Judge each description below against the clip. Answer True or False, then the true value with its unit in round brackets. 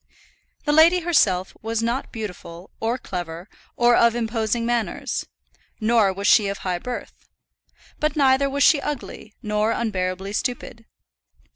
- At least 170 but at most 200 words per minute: False (135 wpm)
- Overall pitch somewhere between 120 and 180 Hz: False (225 Hz)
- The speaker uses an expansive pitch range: False (4.1 semitones)